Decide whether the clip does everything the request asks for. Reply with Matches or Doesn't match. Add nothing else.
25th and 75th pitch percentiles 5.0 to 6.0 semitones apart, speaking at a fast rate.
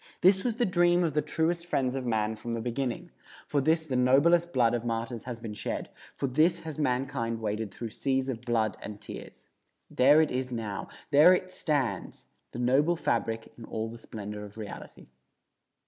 Doesn't match